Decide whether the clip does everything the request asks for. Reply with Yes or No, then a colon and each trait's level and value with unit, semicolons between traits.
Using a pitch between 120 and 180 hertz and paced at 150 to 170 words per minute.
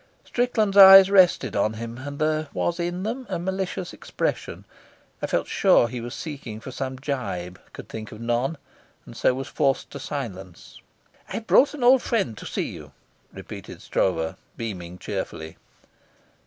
Yes: low, 135 Hz; average, 160 wpm